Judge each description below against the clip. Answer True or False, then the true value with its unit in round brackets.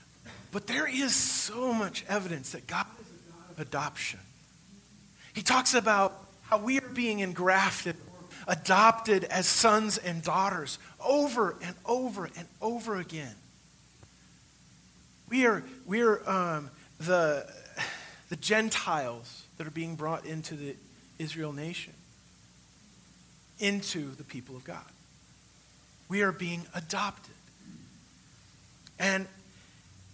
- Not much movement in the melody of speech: False (4.9 semitones)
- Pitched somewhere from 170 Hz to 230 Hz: True (185 Hz)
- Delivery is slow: True (115 wpm)